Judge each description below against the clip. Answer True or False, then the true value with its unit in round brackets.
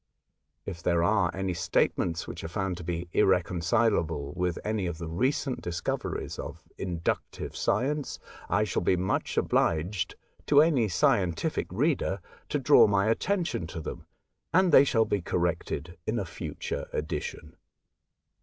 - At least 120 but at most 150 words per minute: True (145 wpm)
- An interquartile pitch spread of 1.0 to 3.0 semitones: False (4.7 semitones)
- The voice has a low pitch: True (95 Hz)